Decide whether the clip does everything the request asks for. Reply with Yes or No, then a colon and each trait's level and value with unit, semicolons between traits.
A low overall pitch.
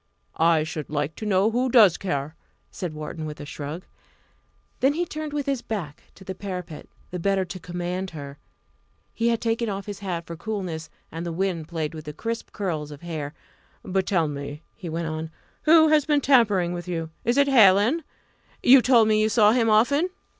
No: medium, 185 Hz